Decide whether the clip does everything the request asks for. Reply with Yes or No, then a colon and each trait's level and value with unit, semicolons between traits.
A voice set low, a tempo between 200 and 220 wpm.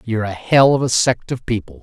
No: low, 115 Hz; fast, 265 wpm